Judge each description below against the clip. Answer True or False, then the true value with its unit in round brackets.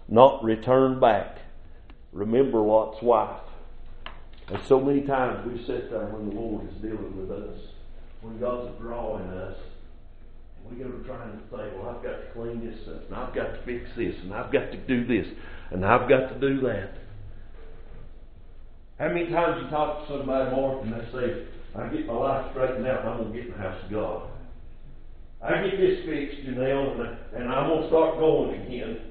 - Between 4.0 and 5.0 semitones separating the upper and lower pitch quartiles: True (4.5 semitones)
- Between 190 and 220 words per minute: True (200 wpm)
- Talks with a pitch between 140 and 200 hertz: False (120 Hz)